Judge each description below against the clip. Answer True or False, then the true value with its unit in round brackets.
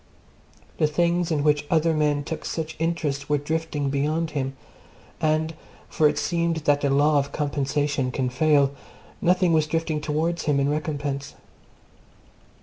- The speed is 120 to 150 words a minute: True (145 wpm)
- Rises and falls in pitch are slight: True (2.1 semitones)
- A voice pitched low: False (150 Hz)